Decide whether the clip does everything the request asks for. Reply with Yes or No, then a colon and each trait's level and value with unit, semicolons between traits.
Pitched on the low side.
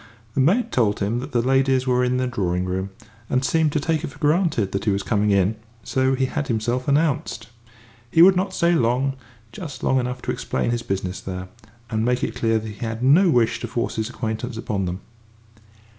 Yes: low, 125 Hz